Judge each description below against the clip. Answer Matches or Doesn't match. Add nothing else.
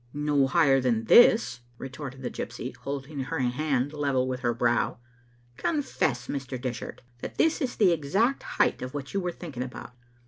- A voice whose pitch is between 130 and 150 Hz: Matches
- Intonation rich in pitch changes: Doesn't match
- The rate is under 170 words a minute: Doesn't match